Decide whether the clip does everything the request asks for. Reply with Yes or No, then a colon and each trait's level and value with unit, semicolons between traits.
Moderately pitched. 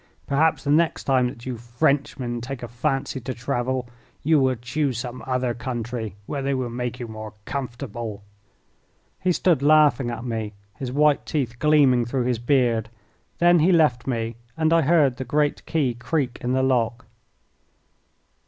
No: low, 130 Hz